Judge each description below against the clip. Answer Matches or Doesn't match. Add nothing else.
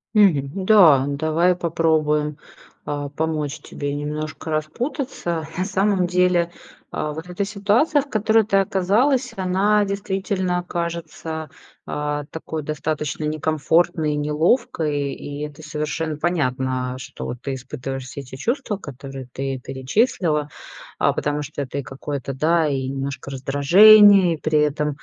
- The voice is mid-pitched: Matches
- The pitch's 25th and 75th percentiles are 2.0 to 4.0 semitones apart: Doesn't match